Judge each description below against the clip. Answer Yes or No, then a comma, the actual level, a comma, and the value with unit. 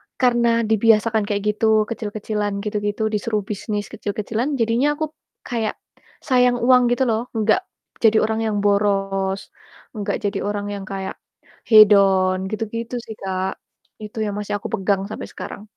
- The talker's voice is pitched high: Yes, high, 215 Hz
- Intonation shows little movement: Yes, narrow, 2.1 semitones